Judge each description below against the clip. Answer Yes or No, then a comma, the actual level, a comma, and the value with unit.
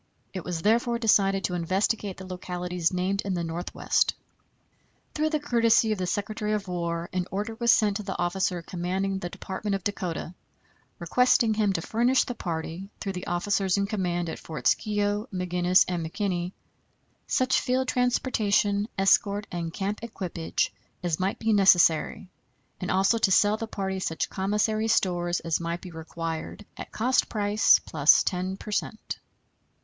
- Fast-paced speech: No, average, 165 wpm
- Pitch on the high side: Yes, high, 195 Hz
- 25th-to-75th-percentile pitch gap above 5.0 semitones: No, average, 3.3 semitones